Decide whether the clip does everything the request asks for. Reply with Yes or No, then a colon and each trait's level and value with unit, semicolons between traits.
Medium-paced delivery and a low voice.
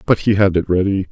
No: fast, 270 wpm; very low, 95 Hz